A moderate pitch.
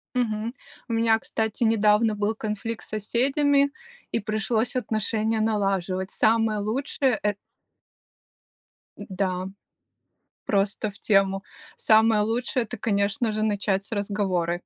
No: high, 215 Hz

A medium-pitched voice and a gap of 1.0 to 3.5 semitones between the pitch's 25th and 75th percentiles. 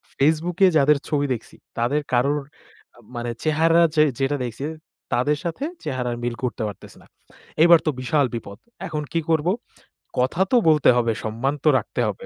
No: medium, 145 Hz; average, 4.4 semitones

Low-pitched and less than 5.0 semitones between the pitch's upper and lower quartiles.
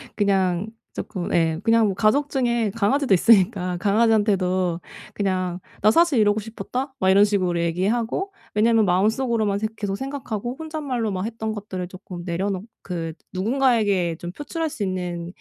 No: high, 205 Hz; average, 4.0 semitones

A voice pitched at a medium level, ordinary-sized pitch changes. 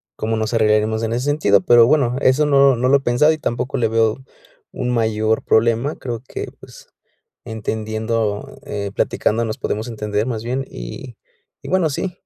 No: low, 115 Hz; average, 3.2 semitones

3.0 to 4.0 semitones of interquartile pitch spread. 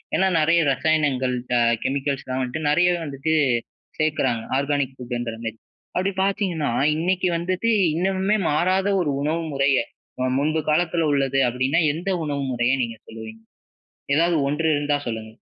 No: average, 4.7 semitones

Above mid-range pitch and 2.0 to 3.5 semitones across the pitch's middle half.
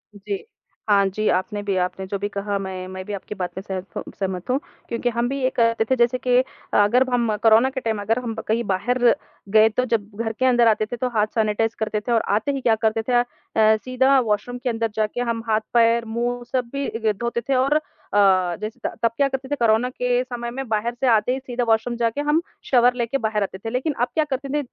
Yes: high, 230 Hz; average, 2.8 semitones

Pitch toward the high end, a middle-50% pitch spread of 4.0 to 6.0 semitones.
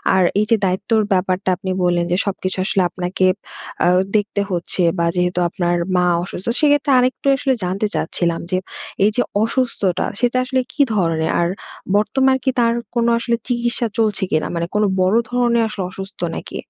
Yes: high, 200 Hz; average, 4.9 semitones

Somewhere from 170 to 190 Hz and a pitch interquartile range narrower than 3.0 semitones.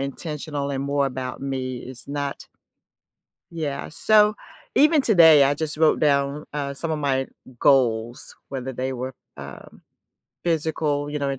No: medium, 140 Hz; narrow, 2.6 semitones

